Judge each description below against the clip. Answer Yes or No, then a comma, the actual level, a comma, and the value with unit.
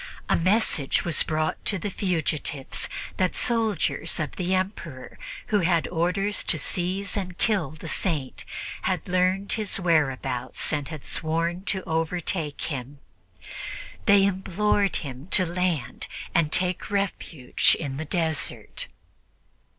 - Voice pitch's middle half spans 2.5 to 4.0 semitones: Yes, average, 3.5 semitones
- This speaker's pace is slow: Yes, slow, 125 wpm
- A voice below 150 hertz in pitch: No, medium, 175 Hz